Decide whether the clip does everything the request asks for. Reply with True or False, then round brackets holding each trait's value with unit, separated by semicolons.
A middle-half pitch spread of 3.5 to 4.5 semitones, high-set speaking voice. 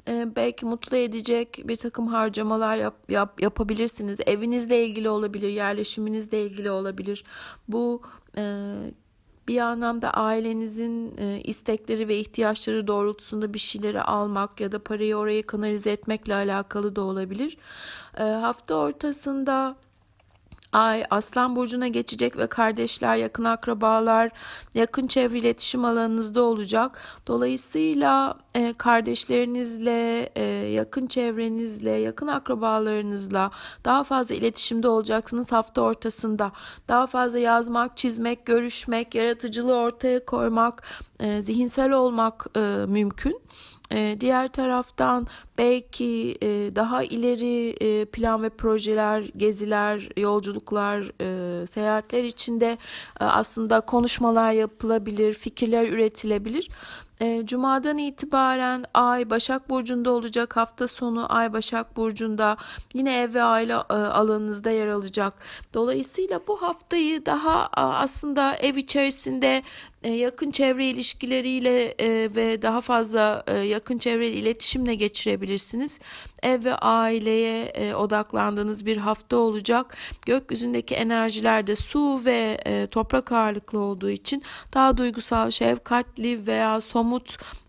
False (2.4 semitones; 225 Hz)